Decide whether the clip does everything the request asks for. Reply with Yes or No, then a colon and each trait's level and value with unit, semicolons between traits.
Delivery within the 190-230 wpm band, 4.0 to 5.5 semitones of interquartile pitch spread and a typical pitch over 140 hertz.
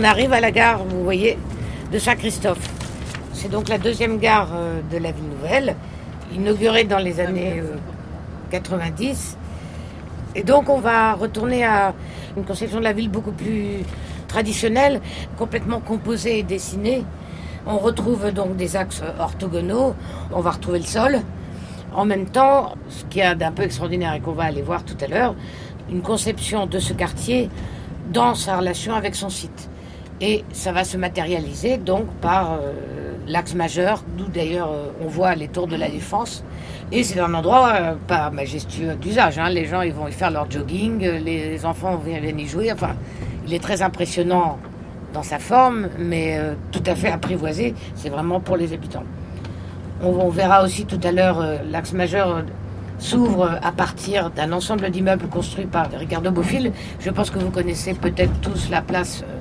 No: average, 175 wpm; average, 4.3 semitones; medium, 185 Hz